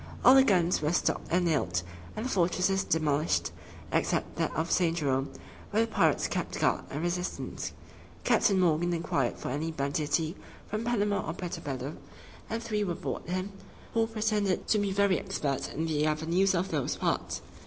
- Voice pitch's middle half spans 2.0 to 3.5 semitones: No, average, 4.6 semitones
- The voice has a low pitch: No, medium, 175 Hz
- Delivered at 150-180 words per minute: Yes, average, 175 wpm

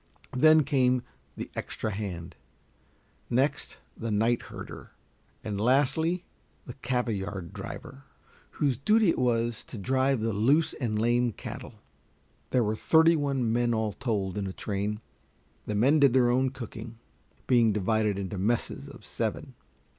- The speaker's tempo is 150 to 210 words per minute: No, average, 140 wpm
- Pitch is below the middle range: Yes, low, 120 Hz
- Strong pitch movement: No, average, 3.8 semitones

